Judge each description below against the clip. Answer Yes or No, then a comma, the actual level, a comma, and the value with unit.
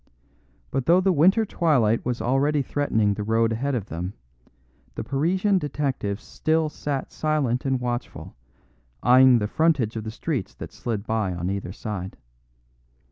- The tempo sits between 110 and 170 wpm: Yes, average, 150 wpm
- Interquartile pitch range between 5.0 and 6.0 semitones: Yes, wide, 5.4 semitones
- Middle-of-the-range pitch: No, low, 125 Hz